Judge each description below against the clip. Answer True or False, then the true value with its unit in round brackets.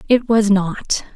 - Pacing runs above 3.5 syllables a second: False (3.4 syllables/s)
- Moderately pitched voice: False (210 Hz)